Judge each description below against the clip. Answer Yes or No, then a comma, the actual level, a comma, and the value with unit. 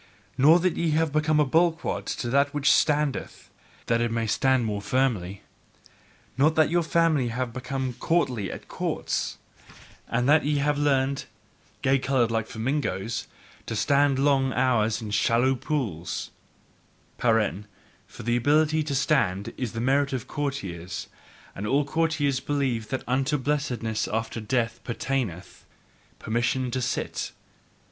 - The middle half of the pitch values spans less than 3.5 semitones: No, average, 4.1 semitones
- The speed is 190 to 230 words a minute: No, average, 140 wpm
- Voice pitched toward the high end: No, low, 130 Hz